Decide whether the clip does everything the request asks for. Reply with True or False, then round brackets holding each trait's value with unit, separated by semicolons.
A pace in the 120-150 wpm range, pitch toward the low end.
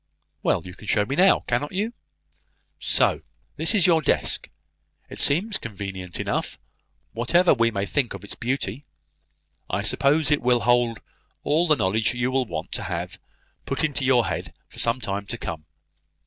False (170 wpm; 125 Hz)